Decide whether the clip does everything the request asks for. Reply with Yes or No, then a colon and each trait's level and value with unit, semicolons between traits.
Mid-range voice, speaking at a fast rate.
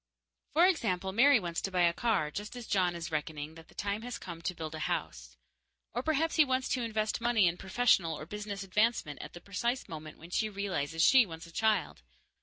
No: high, 195 Hz; fast, 215 wpm